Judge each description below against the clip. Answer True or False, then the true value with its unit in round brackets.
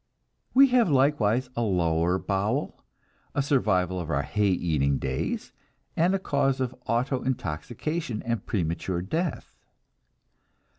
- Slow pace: True (115 wpm)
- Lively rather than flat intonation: True (7.5 semitones)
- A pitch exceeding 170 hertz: False (115 Hz)